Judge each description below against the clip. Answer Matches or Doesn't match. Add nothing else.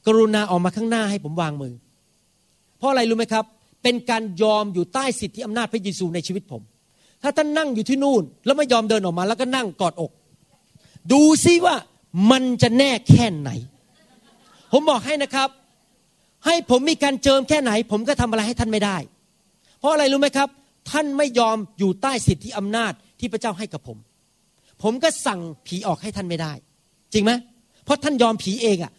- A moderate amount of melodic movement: Doesn't match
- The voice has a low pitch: Doesn't match